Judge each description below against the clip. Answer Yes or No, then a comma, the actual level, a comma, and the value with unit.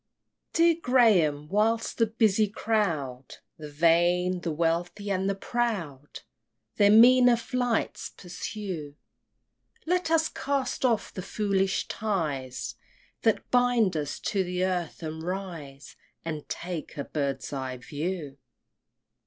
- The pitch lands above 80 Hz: Yes, medium, 185 Hz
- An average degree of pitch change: No, wide, 6.4 semitones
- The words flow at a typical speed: No, slow, 120 wpm